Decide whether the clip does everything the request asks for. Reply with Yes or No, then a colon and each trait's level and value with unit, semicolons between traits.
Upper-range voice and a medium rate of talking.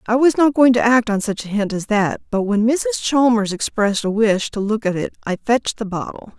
No: high, 225 Hz; fast, 255 wpm